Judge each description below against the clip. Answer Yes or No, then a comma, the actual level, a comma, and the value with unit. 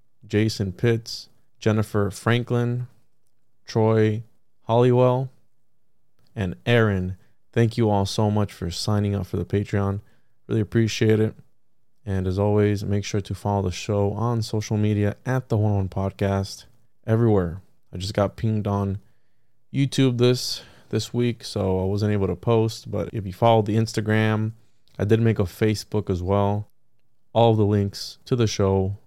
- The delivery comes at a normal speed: Yes, average, 150 wpm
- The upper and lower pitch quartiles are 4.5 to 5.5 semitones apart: No, narrow, 2.5 semitones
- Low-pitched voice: Yes, low, 110 Hz